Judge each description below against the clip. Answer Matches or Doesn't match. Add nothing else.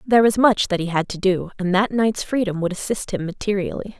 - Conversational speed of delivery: Doesn't match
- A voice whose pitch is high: Matches